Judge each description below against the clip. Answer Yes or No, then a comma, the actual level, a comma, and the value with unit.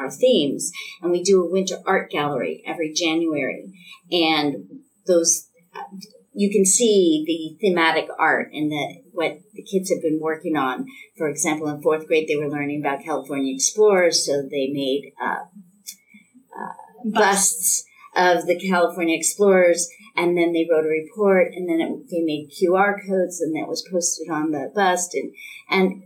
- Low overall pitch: No, medium, 170 Hz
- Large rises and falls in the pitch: No, average, 3.6 semitones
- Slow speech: No, average, 165 wpm